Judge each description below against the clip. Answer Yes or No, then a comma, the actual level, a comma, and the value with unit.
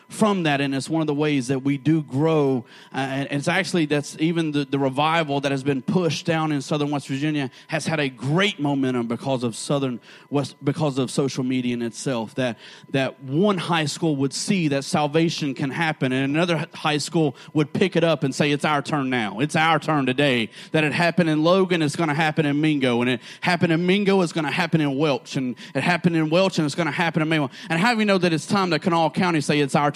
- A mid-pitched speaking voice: Yes, medium, 155 Hz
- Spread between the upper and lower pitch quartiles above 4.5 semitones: No, average, 3.3 semitones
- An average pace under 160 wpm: No, fast, 245 wpm